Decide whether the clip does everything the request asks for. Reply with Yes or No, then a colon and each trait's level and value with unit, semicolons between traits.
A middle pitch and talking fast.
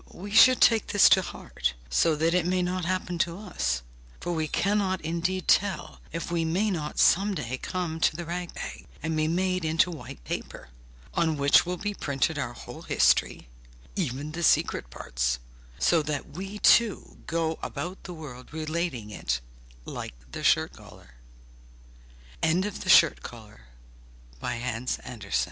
No: medium, 165 Hz; average, 140 wpm